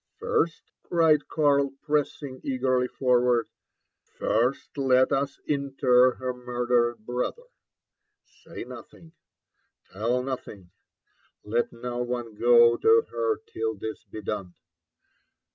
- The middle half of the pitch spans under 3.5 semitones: Yes, average, 2.7 semitones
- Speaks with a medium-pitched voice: No, low, 125 Hz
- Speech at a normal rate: No, slow, 110 wpm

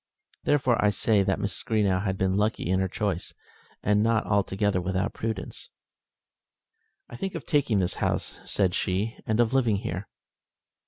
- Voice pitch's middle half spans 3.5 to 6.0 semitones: No, average, 2.8 semitones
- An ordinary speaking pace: Yes, average, 160 wpm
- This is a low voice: Yes, low, 105 Hz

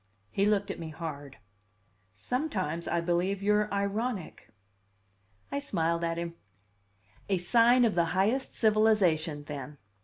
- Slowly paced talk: Yes, slow, 125 wpm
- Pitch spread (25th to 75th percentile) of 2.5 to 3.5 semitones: No, average, 4.3 semitones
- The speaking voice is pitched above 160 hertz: Yes, medium, 185 Hz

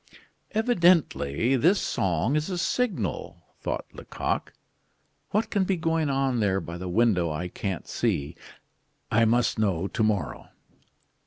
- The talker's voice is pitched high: No, low, 115 Hz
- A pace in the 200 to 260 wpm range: No, slow, 135 wpm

